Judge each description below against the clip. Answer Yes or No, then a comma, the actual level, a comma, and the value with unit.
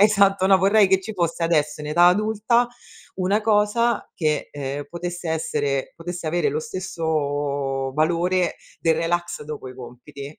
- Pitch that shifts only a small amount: No, average, 4.4 semitones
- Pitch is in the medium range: Yes, medium, 170 Hz